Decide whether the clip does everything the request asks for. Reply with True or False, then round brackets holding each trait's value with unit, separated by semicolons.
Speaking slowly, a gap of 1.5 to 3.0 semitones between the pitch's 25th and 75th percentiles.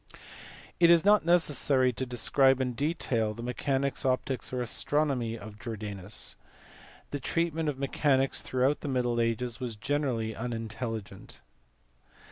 False (125 wpm; 3.8 semitones)